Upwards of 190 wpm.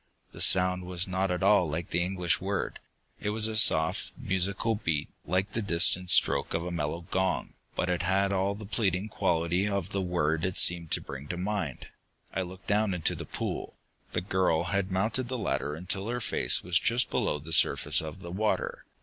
Yes: average, 200 wpm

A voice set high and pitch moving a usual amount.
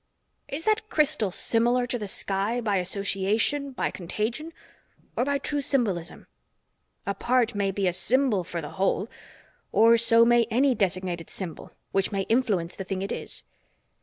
Yes: high, 215 Hz; average, 4.5 semitones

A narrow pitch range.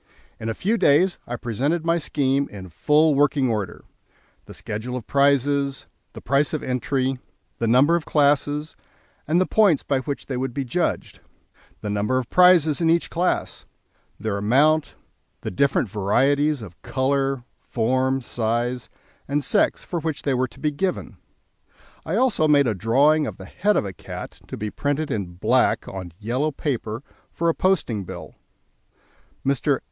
No: average, 4.4 semitones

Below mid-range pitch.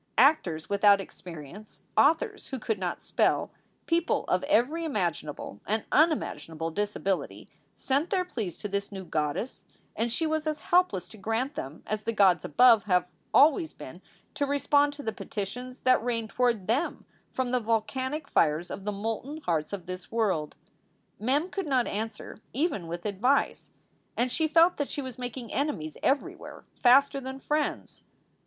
No: high, 230 Hz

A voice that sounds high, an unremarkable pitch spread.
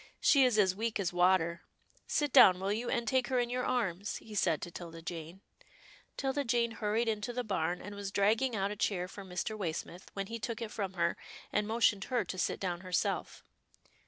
Yes: high, 205 Hz; average, 4.3 semitones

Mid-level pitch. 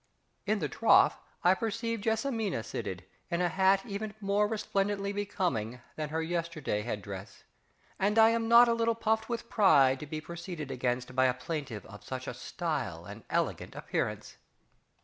Yes: medium, 175 Hz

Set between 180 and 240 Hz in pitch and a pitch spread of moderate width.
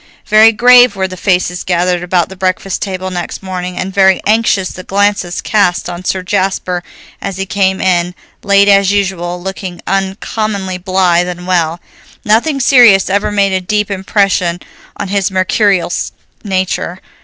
No: high, 190 Hz; narrow, 1.8 semitones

